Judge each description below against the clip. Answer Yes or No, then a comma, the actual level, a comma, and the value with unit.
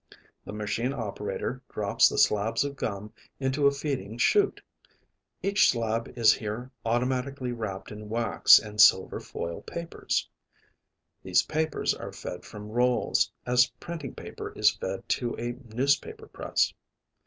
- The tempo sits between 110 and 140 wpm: Yes, slow, 135 wpm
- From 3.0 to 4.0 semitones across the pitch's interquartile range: No, average, 4.6 semitones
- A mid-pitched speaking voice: No, low, 120 Hz